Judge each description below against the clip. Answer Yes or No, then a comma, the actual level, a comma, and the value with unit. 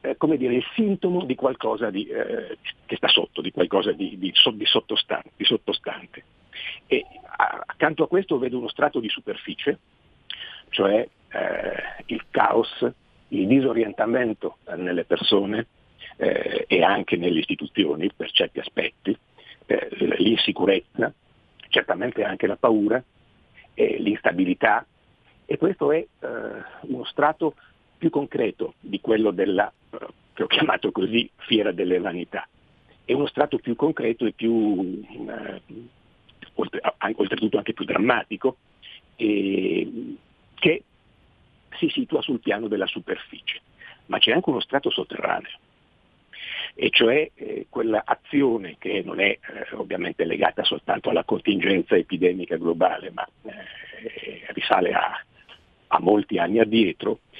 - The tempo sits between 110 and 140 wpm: Yes, average, 130 wpm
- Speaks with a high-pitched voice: Yes, very high, 285 Hz